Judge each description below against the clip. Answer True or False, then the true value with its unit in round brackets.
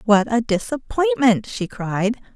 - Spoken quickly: False (130 wpm)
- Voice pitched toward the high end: True (220 Hz)